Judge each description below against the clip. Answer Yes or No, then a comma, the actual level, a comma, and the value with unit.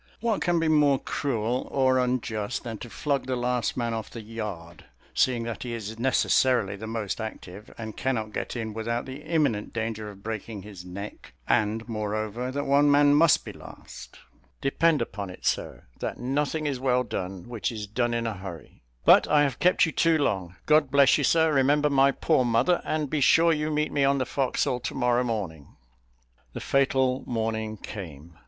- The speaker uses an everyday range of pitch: Yes, average, 4.4 semitones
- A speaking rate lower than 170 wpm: No, average, 190 wpm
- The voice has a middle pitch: No, low, 120 Hz